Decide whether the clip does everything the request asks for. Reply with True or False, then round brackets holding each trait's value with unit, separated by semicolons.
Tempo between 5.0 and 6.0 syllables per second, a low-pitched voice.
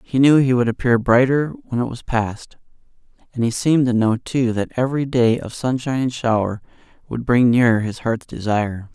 True (5.4 syllables/s; 120 Hz)